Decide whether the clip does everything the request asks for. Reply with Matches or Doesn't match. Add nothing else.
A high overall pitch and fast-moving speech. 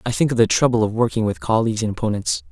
Doesn't match